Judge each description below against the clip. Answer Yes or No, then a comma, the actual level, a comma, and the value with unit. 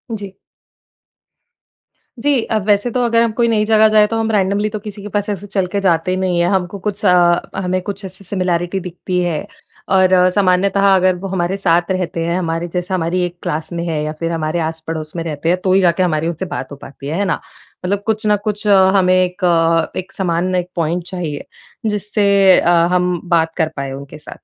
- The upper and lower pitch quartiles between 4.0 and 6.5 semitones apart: No, average, 2.9 semitones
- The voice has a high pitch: No, medium, 180 Hz